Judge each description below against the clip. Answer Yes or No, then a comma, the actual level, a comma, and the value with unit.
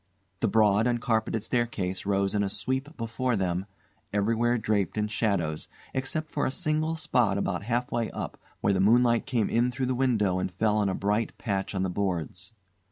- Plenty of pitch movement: No, average, 3.7 semitones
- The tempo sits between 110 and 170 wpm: No, average, 185 wpm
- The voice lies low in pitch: Yes, low, 110 Hz